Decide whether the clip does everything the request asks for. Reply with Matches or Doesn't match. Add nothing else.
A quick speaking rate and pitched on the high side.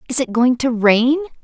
Matches